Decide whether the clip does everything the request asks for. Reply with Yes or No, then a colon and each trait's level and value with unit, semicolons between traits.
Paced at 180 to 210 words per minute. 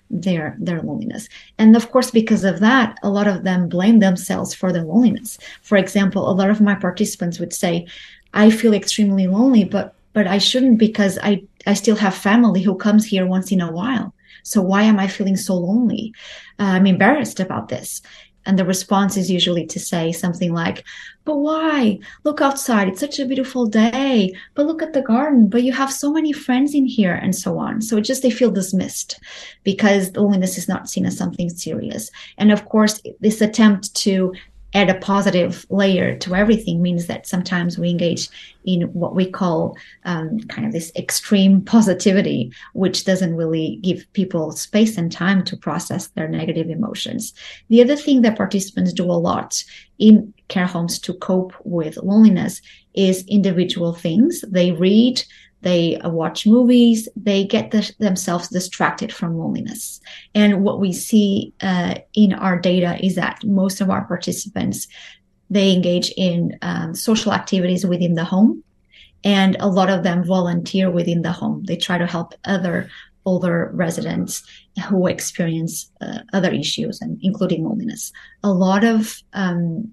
No: average, 170 wpm